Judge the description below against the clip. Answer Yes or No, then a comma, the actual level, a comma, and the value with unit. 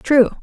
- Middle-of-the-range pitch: No, very high, 260 Hz